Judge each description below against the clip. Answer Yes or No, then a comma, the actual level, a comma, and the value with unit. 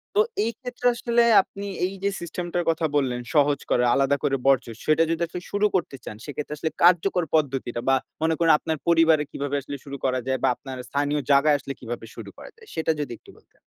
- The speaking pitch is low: No, medium, 150 Hz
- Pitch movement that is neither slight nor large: Yes, average, 3.8 semitones